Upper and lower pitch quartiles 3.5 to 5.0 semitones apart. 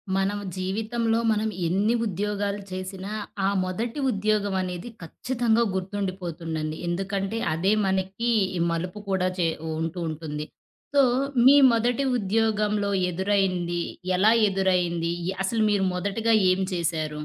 No: average, 2.9 semitones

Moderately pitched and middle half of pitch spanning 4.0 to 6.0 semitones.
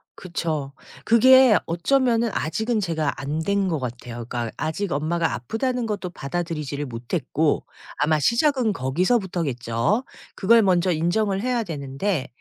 No: medium, 170 Hz; wide, 7.3 semitones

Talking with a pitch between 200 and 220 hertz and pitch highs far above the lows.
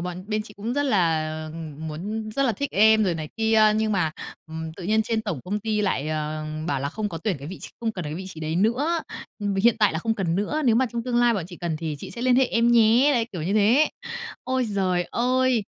Yes: high, 210 Hz; wide, 5.8 semitones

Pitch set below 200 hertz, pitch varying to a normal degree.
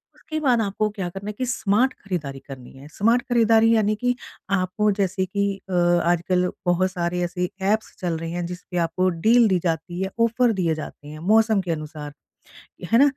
Yes: high, 190 Hz; average, 4.3 semitones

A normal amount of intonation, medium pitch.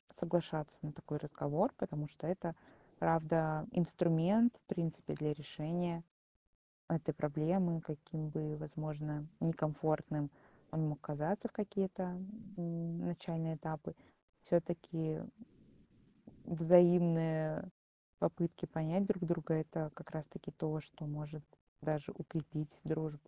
No: narrow, 2.0 semitones; medium, 160 Hz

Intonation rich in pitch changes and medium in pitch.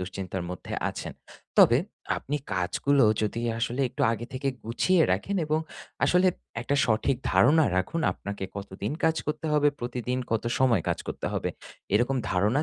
No: wide, 6.3 semitones; low, 120 Hz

